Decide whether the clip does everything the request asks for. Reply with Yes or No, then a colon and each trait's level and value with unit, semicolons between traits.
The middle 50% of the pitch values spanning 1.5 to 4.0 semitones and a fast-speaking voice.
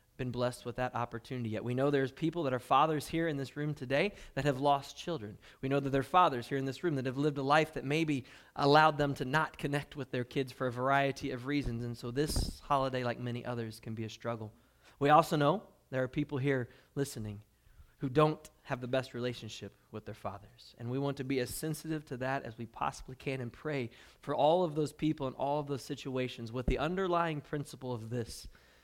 Yes: average, 3.2 semitones; fast, 230 wpm